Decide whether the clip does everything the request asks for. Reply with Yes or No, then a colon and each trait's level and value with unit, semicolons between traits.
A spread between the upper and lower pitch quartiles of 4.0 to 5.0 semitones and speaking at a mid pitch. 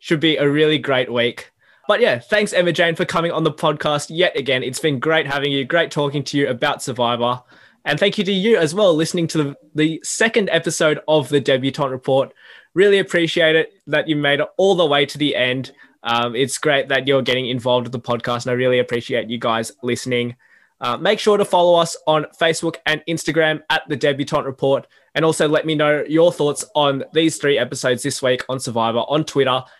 No: average, 3.6 semitones; medium, 150 Hz